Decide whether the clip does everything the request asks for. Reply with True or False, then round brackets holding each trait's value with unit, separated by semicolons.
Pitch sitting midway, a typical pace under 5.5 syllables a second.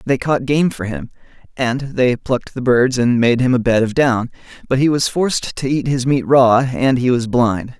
False (125 Hz; 4.7 syllables/s)